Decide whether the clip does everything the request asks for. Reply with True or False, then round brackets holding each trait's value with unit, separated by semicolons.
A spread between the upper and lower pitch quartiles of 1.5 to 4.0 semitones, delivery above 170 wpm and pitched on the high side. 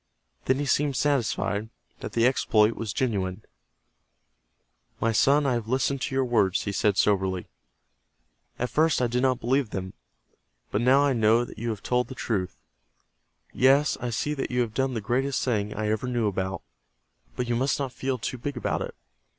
False (3.7 semitones; 185 wpm; 120 Hz)